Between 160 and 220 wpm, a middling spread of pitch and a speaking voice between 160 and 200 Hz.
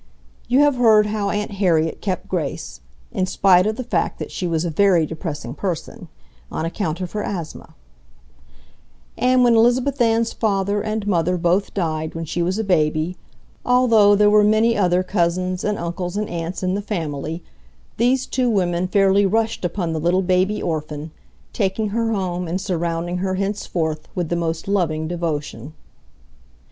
Yes: average, 165 wpm; average, 3.8 semitones; medium, 185 Hz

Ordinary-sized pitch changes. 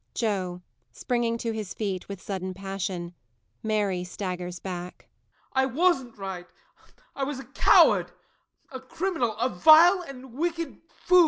No: wide, 6.3 semitones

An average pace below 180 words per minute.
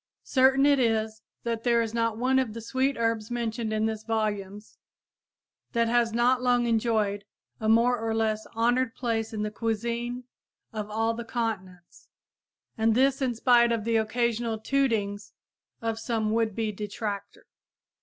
Yes: average, 155 wpm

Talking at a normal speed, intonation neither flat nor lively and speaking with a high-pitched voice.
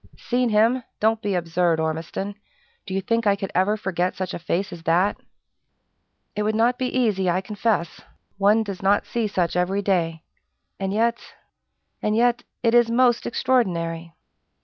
Yes: average, 165 wpm; average, 4.2 semitones; high, 200 Hz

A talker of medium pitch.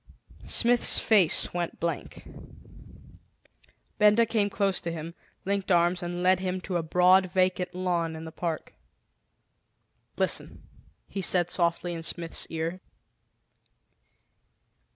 Yes: medium, 180 Hz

